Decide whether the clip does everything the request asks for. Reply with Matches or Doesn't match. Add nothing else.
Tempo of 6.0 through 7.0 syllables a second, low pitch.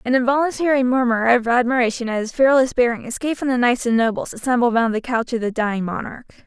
Doesn't match